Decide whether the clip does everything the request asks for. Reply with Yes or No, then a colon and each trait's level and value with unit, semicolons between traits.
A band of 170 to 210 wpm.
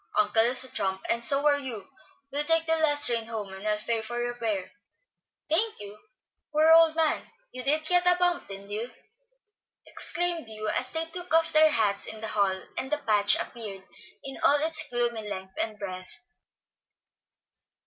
Yes: average, 180 wpm